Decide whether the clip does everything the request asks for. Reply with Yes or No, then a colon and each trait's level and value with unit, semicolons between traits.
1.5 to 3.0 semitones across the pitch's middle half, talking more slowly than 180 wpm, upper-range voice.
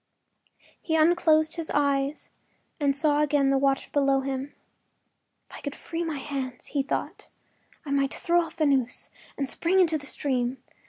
Yes: narrow, 2.4 semitones; average, 165 wpm; very high, 285 Hz